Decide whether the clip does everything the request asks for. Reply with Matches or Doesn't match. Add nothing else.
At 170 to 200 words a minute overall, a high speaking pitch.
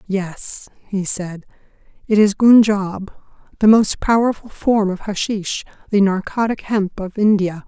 Doesn't match